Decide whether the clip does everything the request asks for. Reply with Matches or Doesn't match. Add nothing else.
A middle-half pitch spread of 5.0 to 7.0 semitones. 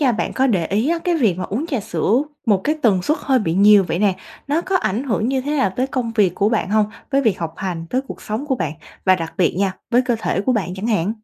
Matches